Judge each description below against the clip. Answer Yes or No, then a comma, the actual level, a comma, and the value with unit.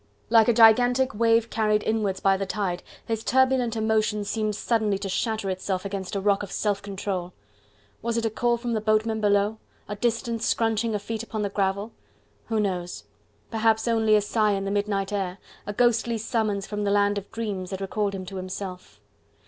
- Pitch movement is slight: Yes, narrow, 2.3 semitones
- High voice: Yes, high, 210 Hz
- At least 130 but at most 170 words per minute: No, average, 190 wpm